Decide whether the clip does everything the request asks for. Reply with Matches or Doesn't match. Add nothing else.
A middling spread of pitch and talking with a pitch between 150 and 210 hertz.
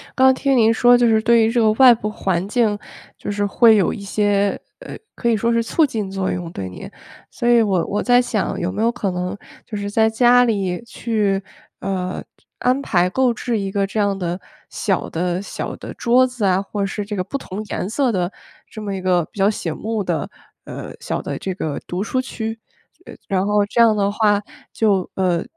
Matches